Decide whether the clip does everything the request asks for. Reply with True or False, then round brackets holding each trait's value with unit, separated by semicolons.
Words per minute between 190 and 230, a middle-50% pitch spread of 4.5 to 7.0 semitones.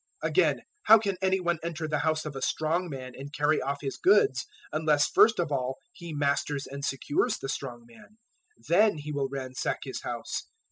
False (195 wpm; 3.8 semitones)